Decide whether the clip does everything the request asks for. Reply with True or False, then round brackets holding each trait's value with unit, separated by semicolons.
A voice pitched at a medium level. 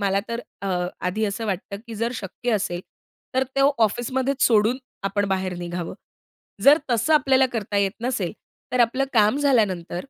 False (215 Hz)